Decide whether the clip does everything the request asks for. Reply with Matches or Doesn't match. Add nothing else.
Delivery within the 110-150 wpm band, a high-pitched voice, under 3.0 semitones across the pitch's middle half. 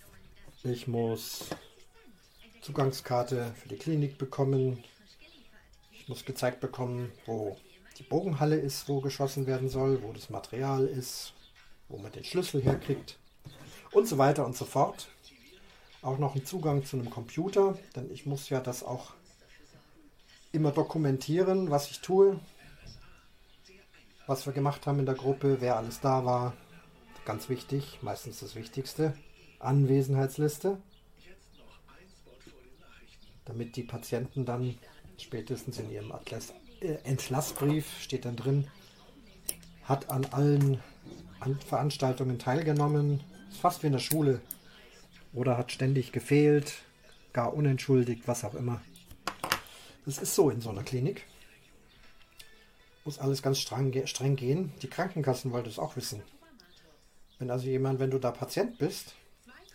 Doesn't match